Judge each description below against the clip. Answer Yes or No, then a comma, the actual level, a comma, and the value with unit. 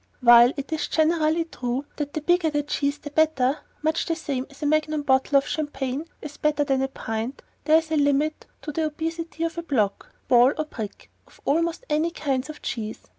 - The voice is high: Yes, very high, 295 Hz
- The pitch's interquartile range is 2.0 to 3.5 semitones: Yes, average, 2.8 semitones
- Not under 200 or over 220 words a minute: Yes, fast, 205 wpm